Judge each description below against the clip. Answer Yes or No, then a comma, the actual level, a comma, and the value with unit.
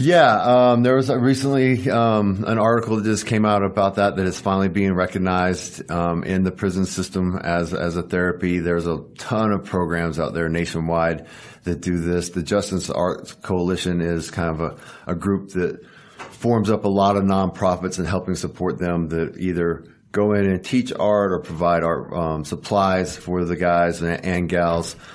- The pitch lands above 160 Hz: No, very low, 90 Hz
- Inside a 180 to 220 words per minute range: Yes, average, 190 wpm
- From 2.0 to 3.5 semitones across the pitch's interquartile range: Yes, average, 2.8 semitones